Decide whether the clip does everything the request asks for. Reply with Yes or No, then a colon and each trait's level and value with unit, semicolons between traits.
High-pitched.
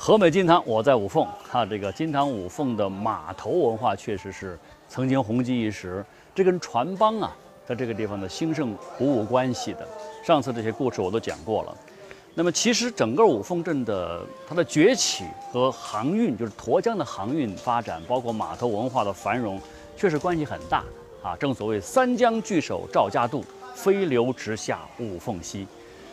No: low, 125 Hz